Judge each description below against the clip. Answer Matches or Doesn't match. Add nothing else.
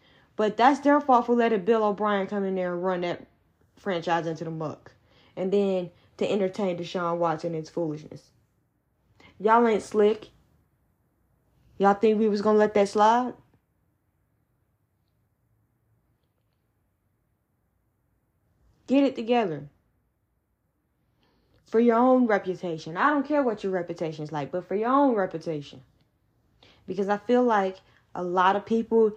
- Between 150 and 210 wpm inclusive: Doesn't match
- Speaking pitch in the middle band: Matches